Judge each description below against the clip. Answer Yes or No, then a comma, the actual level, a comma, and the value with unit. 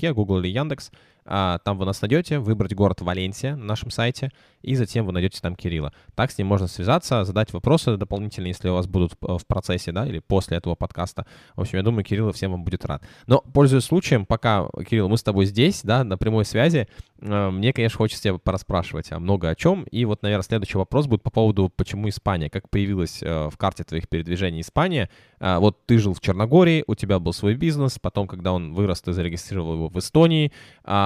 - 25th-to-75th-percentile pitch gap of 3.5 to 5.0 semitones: Yes, average, 4.4 semitones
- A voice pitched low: Yes, low, 100 Hz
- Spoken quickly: Yes, fast, 205 wpm